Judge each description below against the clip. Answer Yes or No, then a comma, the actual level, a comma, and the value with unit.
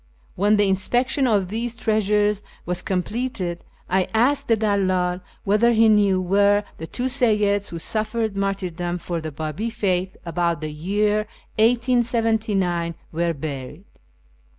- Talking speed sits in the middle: No, slow, 130 wpm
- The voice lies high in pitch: Yes, high, 200 Hz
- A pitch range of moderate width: Yes, average, 3.8 semitones